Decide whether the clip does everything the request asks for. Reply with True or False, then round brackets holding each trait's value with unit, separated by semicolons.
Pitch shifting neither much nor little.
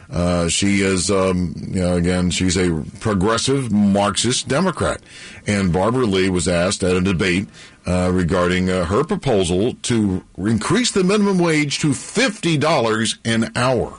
True (4.8 semitones)